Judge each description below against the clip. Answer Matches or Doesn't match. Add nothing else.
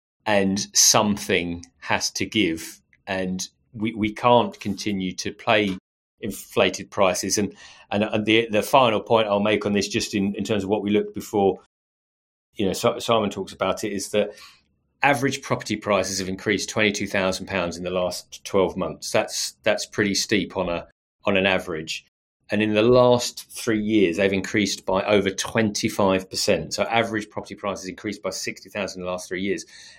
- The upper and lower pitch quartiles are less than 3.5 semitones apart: Matches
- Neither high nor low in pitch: Doesn't match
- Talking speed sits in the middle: Matches